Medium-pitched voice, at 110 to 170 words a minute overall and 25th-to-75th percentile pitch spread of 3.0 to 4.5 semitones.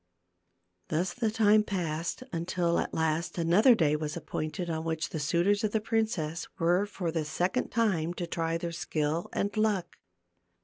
Yes: medium, 170 Hz; average, 165 wpm; average, 4.1 semitones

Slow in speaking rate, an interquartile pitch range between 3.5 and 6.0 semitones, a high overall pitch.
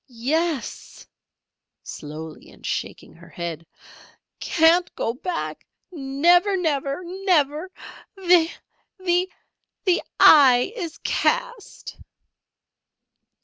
Yes: slow, 80 wpm; average, 5.1 semitones; very high, 325 Hz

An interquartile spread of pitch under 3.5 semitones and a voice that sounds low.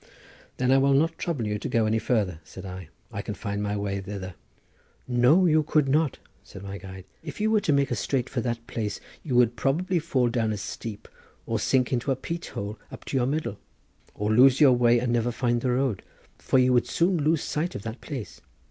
No: average, 4.8 semitones; low, 125 Hz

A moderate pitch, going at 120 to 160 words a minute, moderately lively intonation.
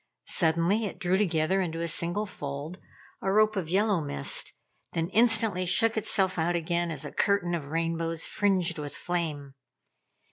Yes: medium, 175 Hz; average, 155 wpm; average, 3.1 semitones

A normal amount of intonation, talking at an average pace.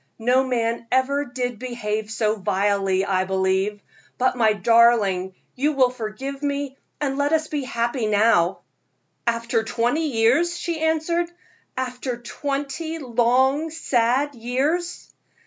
No: average, 4.2 semitones; slow, 125 wpm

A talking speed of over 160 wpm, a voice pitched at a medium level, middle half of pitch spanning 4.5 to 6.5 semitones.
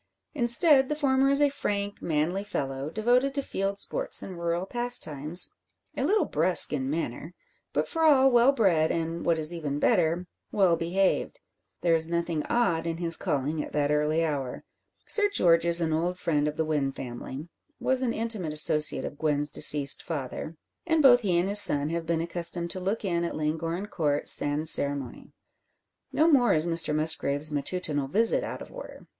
Yes: average, 180 wpm; medium, 170 Hz; wide, 5.4 semitones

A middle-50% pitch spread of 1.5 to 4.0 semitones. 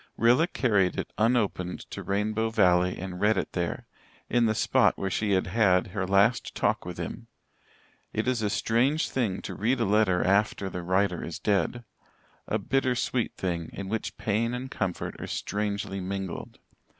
Yes: average, 3.4 semitones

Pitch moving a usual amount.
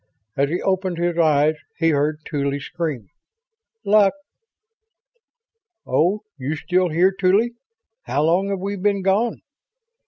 Yes: average, 4.3 semitones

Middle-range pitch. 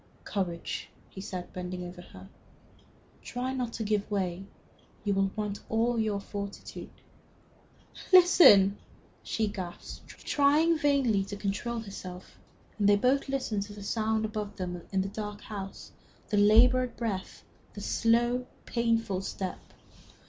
No: high, 210 Hz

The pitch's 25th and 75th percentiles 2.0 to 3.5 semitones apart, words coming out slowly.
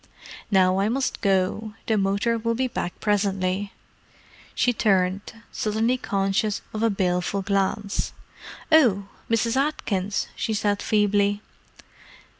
Yes: narrow, 2.5 semitones; slow, 110 wpm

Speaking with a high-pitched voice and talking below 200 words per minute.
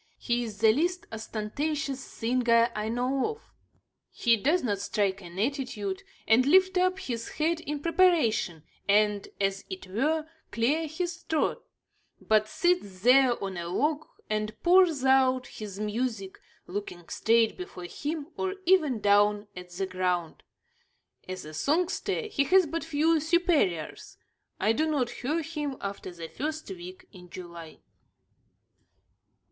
Yes: high, 240 Hz; average, 140 wpm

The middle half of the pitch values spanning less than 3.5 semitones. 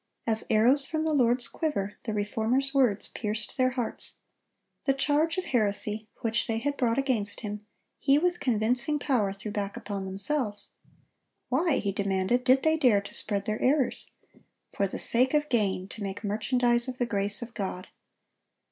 No: average, 4.7 semitones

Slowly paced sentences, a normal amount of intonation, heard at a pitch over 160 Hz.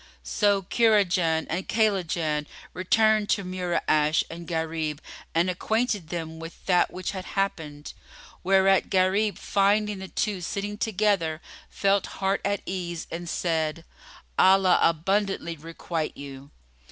Yes: slow, 120 wpm; average, 3.4 semitones; medium, 185 Hz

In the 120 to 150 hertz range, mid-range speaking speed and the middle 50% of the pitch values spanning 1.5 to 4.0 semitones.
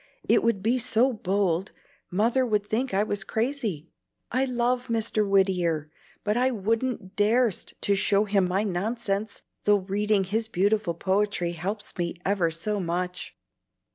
No: high, 205 Hz; average, 145 wpm; average, 3.1 semitones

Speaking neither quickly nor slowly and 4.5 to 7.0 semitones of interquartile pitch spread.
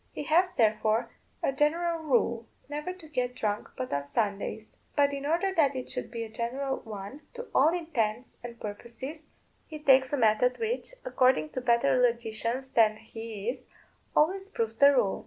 Yes: average, 175 wpm; average, 4.9 semitones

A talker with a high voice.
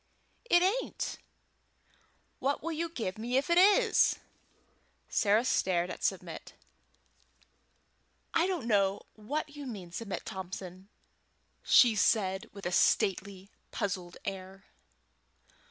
Yes: high, 210 Hz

